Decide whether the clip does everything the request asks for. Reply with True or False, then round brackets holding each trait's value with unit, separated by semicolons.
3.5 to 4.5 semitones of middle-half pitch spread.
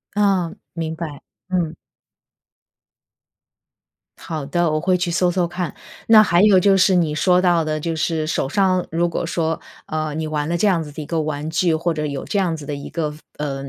False (2.6 semitones)